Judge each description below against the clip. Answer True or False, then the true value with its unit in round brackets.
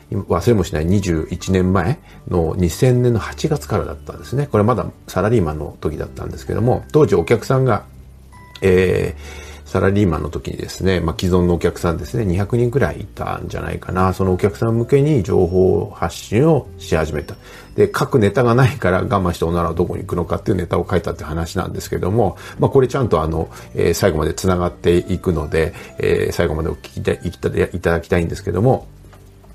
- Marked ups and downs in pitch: False (3.7 semitones)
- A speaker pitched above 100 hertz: False (95 Hz)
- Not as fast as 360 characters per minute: False (400 characters per minute)